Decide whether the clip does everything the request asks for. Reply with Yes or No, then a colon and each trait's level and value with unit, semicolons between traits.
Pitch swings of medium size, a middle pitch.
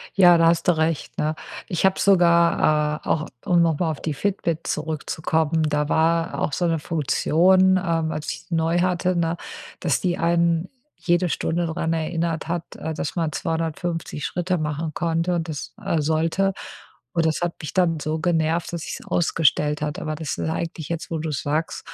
No: narrow, 1.7 semitones; medium, 165 Hz